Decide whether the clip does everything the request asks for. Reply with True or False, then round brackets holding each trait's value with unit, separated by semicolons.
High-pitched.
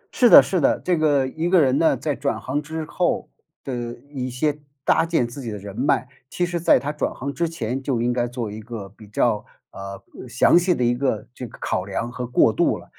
False (130 Hz)